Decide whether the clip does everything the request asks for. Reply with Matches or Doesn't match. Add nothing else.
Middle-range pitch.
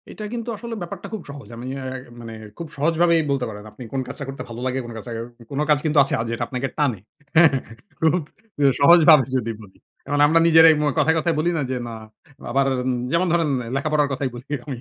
Matches